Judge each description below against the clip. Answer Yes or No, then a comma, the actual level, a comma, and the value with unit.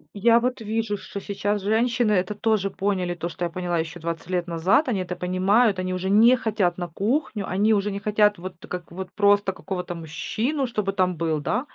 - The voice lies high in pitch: Yes, high, 195 Hz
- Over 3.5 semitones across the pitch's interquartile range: No, average, 3.1 semitones